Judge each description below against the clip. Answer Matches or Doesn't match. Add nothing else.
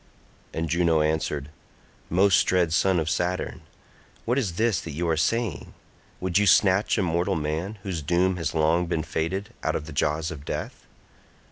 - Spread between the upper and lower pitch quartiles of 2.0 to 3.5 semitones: Matches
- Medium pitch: Doesn't match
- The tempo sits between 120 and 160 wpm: Doesn't match